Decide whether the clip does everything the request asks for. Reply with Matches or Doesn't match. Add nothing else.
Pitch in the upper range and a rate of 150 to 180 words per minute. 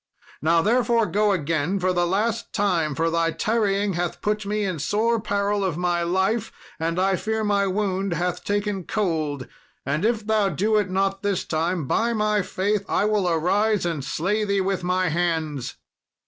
Matches